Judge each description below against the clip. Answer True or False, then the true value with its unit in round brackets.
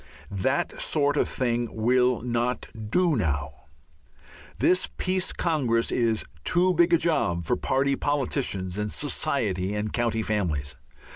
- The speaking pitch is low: True (120 Hz)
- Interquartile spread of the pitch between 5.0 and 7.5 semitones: True (5.6 semitones)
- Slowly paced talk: True (130 wpm)